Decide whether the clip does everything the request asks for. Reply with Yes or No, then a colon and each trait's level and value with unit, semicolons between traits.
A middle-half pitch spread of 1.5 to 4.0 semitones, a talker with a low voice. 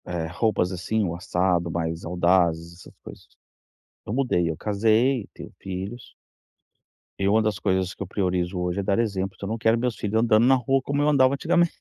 No: average, 4.5 semitones; low, 100 Hz